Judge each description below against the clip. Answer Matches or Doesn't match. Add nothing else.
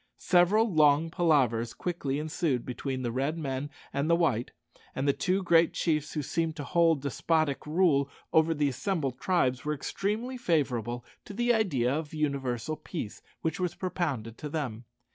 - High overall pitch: Doesn't match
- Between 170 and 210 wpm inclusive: Doesn't match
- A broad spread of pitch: Doesn't match